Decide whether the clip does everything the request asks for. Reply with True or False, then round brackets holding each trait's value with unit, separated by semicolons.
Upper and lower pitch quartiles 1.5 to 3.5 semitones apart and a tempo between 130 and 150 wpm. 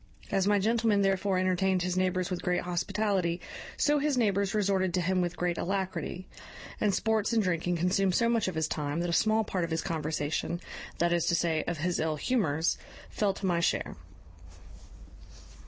False (2.7 semitones; 185 wpm)